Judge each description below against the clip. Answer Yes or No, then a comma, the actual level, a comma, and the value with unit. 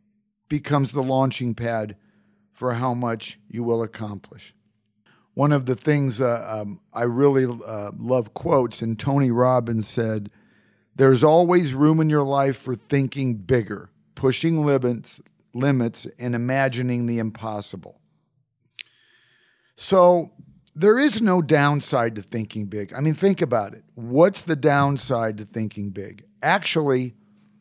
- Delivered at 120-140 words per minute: Yes, slow, 135 wpm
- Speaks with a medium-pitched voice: No, low, 125 Hz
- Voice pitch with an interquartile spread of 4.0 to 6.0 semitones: Yes, average, 4.5 semitones